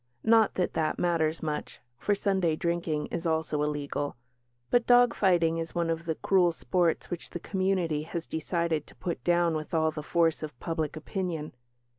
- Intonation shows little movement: Yes, narrow, 2.1 semitones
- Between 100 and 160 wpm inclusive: No, average, 175 wpm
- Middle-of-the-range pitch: Yes, medium, 165 Hz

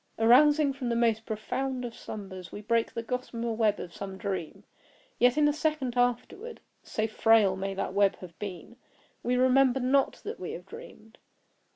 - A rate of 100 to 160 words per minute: No, average, 175 wpm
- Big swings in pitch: No, average, 4.1 semitones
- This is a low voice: No, high, 235 Hz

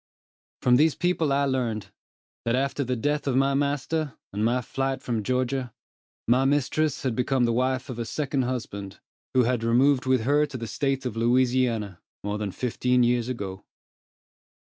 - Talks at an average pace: Yes, average, 170 wpm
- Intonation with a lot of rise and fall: No, average, 2.7 semitones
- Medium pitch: No, low, 125 Hz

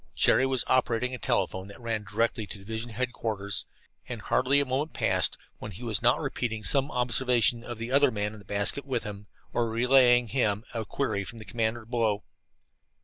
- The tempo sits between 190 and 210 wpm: Yes, average, 195 wpm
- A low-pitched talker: Yes, low, 115 Hz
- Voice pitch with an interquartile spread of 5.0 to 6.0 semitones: No, average, 2.9 semitones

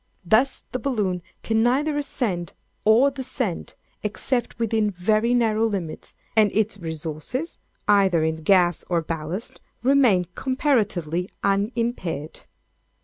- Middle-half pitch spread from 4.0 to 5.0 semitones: No, wide, 5.6 semitones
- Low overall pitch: No, high, 210 Hz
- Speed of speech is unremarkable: No, slow, 110 wpm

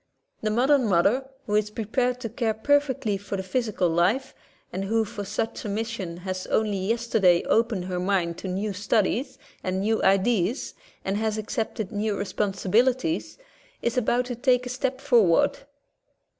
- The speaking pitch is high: Yes, high, 215 Hz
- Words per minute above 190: No, average, 160 wpm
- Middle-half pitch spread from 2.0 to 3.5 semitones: No, average, 4.0 semitones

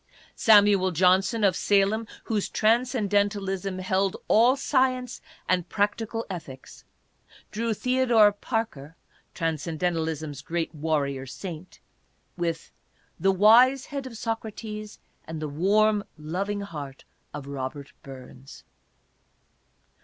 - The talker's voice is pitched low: No, high, 195 Hz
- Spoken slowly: Yes, slow, 110 wpm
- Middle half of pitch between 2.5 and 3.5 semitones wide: No, average, 5.3 semitones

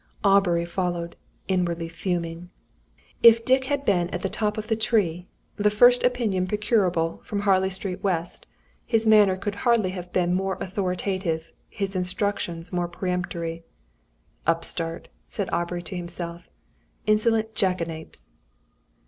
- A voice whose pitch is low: No, medium, 185 Hz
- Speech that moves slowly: Yes, slow, 130 wpm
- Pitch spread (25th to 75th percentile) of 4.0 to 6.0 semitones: No, average, 3.3 semitones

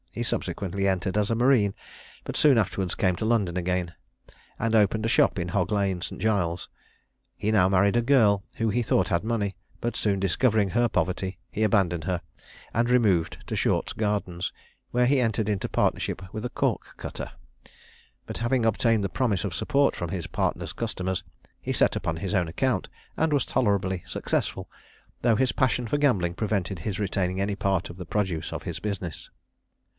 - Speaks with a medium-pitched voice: No, low, 100 Hz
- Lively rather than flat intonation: No, average, 3.7 semitones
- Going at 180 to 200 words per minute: Yes, average, 185 wpm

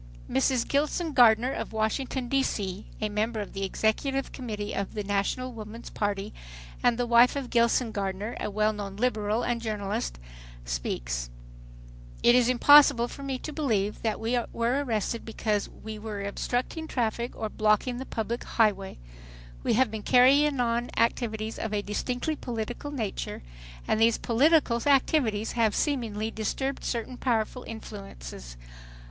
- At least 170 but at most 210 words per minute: No, average, 155 wpm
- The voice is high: Yes, high, 225 Hz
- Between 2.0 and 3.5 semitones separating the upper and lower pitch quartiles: Yes, average, 3.1 semitones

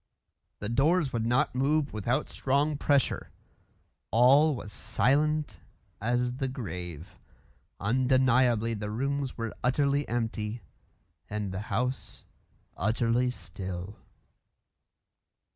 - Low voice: Yes, low, 120 Hz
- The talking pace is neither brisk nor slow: No, slow, 95 wpm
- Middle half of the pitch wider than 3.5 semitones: Yes, average, 4.3 semitones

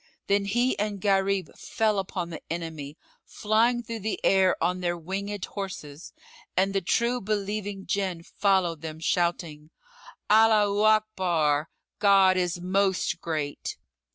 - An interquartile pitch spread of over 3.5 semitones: No, average, 3.2 semitones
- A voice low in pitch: No, high, 195 Hz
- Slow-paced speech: Yes, slow, 125 wpm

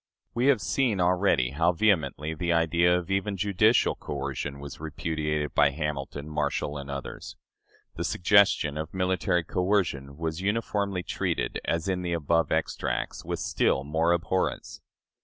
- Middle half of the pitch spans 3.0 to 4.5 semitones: Yes, average, 4.1 semitones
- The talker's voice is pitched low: Yes, very low, 85 Hz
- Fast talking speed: No, average, 145 wpm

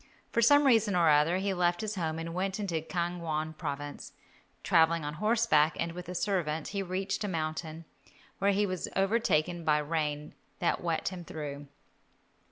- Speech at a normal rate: Yes, average, 175 wpm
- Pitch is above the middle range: No, medium, 170 Hz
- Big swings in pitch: No, average, 3.8 semitones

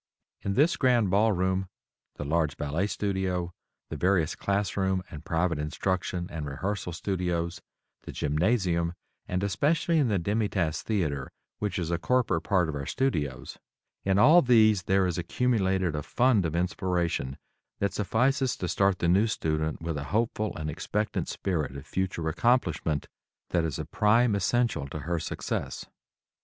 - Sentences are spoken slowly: No, average, 155 wpm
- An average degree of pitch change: Yes, average, 4.2 semitones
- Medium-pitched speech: No, very low, 95 Hz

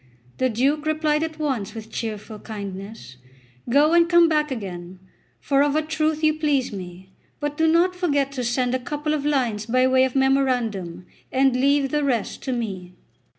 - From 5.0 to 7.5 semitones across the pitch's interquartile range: Yes, wide, 5.5 semitones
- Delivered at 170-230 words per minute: Yes, average, 180 wpm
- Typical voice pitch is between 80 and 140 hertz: No, very high, 265 Hz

